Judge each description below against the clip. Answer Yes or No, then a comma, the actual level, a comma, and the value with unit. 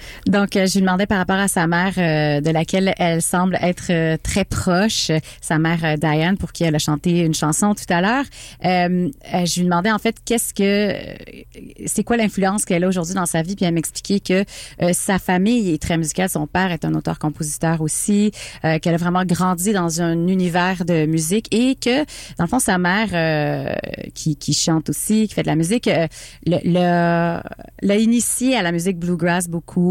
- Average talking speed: Yes, average, 200 wpm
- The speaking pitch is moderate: Yes, medium, 175 Hz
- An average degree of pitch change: Yes, average, 3.3 semitones